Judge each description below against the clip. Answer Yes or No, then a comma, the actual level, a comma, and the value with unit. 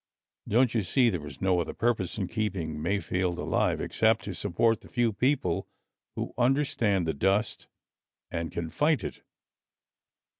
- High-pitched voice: No, low, 100 Hz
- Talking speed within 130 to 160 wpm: Yes, average, 150 wpm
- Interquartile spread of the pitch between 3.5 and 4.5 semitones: No, average, 5.0 semitones